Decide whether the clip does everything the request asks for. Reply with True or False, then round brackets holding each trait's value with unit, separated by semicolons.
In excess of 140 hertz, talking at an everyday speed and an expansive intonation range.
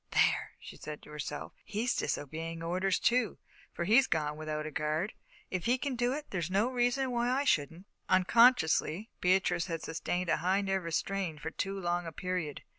True (185 Hz; 185 wpm; 5.9 semitones)